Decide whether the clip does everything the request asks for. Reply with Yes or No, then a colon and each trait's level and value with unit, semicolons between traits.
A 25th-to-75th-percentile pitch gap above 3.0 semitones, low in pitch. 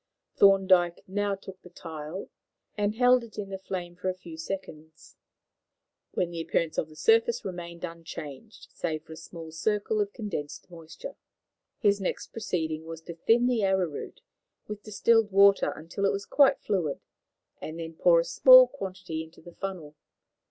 No: average, 4.0 semitones; medium, 185 Hz